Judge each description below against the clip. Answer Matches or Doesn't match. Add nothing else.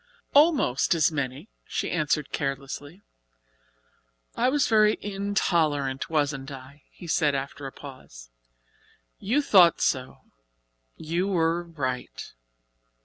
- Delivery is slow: Matches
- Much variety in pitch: Matches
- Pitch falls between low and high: Matches